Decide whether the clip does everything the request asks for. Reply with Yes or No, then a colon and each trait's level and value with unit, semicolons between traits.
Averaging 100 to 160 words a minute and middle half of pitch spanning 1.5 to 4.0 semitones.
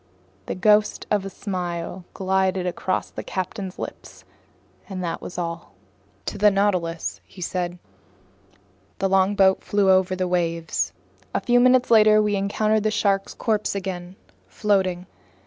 Yes: average, 140 wpm; narrow, 2.4 semitones